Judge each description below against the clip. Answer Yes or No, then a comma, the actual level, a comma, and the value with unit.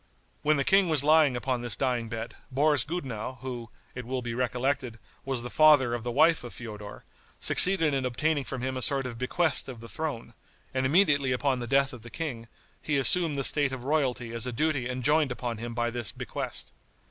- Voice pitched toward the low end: Yes, low, 130 Hz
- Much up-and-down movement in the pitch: No, average, 3.4 semitones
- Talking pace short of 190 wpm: No, fast, 205 wpm